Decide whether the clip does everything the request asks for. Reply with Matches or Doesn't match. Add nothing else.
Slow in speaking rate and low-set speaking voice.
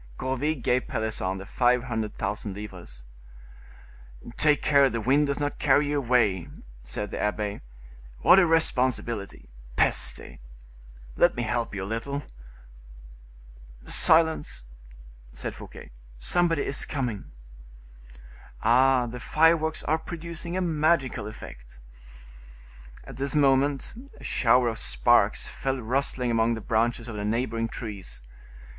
Matches